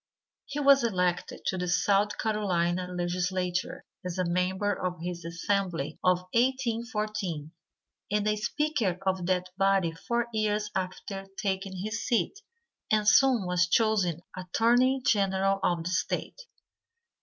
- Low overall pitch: No, high, 195 Hz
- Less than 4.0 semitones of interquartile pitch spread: Yes, average, 3.1 semitones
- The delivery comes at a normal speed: No, slow, 130 wpm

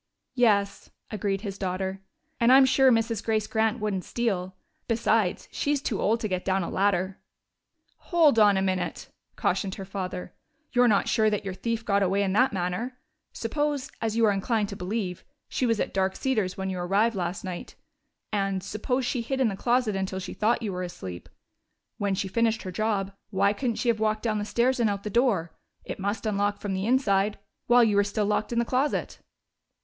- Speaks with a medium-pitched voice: No, high, 210 Hz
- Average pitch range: Yes, average, 3.3 semitones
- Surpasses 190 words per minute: Yes, fast, 205 wpm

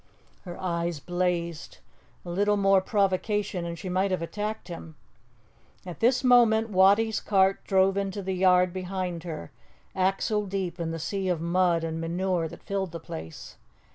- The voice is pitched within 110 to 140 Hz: No, medium, 185 Hz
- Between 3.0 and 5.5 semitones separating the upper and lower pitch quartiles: No, narrow, 2.6 semitones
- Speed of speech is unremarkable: Yes, average, 160 wpm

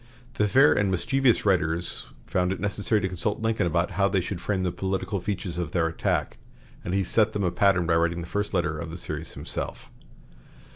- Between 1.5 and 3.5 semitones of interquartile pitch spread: Yes, average, 3.0 semitones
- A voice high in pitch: No, very low, 95 Hz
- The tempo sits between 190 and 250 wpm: Yes, fast, 205 wpm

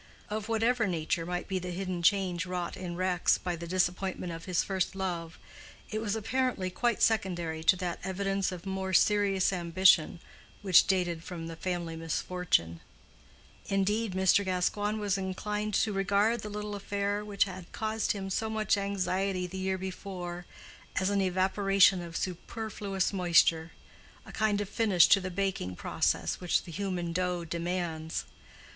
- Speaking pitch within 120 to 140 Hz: No, high, 190 Hz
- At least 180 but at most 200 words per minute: No, average, 155 wpm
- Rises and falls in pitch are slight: Yes, narrow, 2.3 semitones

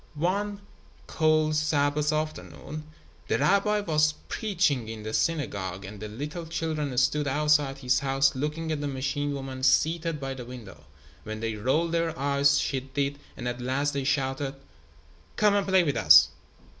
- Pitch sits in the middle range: Yes, medium, 145 Hz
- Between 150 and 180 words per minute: Yes, average, 160 wpm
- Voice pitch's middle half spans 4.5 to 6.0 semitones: No, average, 3.2 semitones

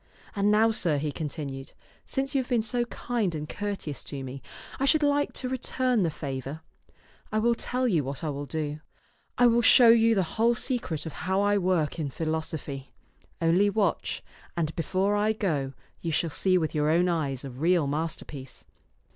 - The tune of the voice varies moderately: No, wide, 6.9 semitones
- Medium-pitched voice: Yes, medium, 175 Hz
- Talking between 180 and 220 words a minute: Yes, average, 185 wpm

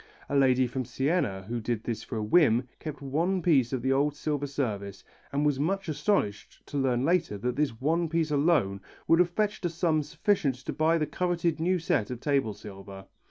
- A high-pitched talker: No, medium, 140 Hz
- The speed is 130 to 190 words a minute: No, fast, 205 wpm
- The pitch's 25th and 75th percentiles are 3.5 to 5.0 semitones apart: No, wide, 5.4 semitones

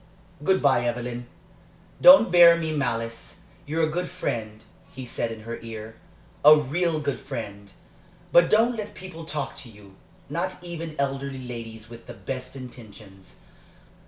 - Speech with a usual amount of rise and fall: No, wide, 6.4 semitones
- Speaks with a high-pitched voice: No, low, 135 Hz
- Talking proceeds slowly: No, average, 150 wpm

